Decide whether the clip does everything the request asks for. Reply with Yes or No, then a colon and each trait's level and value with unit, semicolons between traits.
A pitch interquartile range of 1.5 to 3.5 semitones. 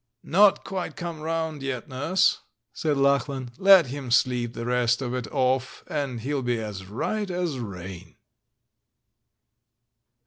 No: average, 4.8 semitones